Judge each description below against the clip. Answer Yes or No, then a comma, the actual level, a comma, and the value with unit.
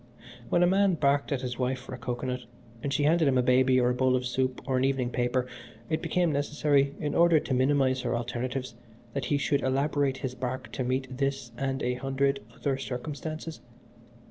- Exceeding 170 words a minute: Yes, average, 200 wpm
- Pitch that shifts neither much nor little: No, narrow, 2.1 semitones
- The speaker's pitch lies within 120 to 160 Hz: Yes, low, 135 Hz